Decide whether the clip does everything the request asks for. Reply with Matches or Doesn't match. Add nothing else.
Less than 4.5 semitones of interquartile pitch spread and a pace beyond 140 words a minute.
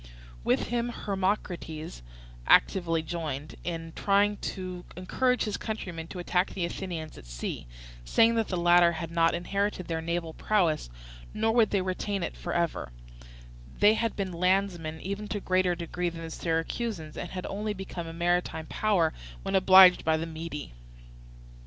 Matches